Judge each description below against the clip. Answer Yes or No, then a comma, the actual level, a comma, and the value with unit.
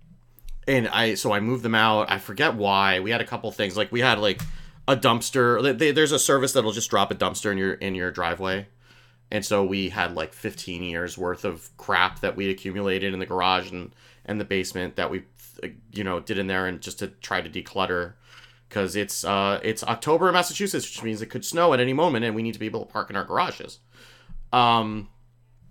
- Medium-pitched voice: No, low, 105 Hz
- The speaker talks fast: Yes, fast, 225 wpm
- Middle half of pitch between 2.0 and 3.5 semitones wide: No, average, 4.2 semitones